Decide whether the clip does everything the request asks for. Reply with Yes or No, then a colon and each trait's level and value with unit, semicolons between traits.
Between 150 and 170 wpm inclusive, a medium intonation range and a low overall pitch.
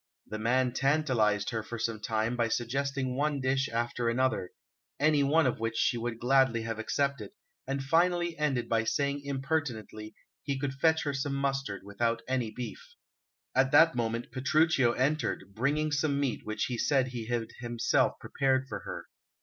Yes: average, 165 wpm; average, 3.4 semitones; low, 130 Hz